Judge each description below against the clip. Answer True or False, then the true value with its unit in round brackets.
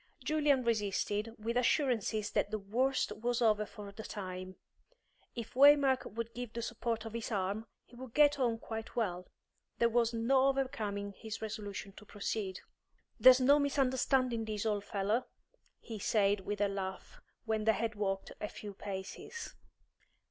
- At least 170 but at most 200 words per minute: False (155 wpm)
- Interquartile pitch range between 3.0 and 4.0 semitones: True (3.4 semitones)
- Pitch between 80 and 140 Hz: False (225 Hz)